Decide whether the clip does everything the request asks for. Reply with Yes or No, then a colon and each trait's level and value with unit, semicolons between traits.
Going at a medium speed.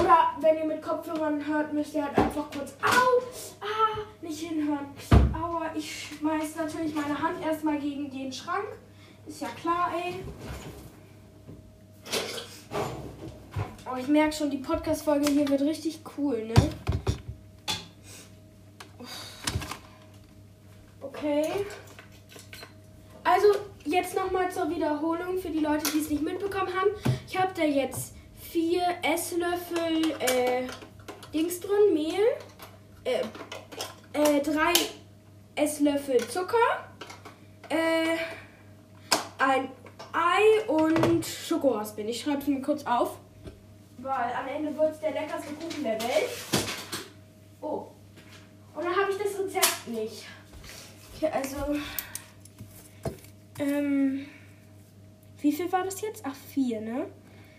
No: slow, 115 wpm